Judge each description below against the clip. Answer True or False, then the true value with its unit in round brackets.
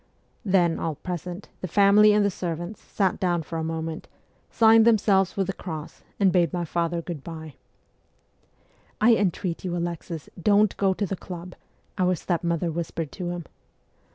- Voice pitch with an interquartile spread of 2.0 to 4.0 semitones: True (2.7 semitones)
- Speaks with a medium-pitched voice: True (175 Hz)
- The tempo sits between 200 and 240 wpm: False (165 wpm)